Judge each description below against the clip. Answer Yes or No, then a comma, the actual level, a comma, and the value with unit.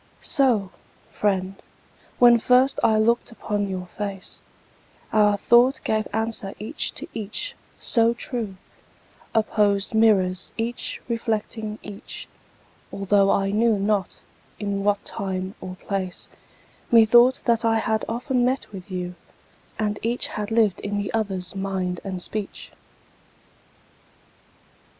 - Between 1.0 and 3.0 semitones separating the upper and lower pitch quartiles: Yes, average, 2.7 semitones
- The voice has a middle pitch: No, high, 210 Hz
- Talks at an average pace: No, slow, 120 wpm